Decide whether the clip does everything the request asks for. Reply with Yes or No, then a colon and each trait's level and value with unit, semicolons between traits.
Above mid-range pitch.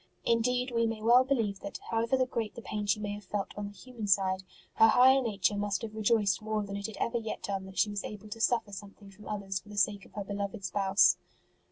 Yes: high, 210 Hz